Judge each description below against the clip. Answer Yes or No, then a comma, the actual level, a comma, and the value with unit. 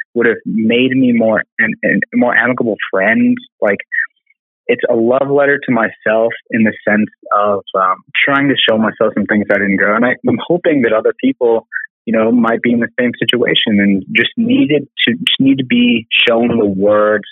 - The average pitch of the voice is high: No, low, 120 Hz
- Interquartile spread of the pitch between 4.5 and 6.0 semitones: Yes, average, 5.0 semitones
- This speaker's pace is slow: No, average, 200 wpm